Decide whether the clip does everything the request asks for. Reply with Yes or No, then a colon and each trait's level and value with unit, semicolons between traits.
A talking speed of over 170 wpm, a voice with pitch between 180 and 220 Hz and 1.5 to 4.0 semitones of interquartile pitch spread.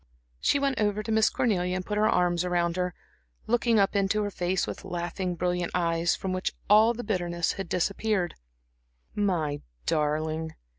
No: average, 160 wpm; medium, 185 Hz; average, 3.3 semitones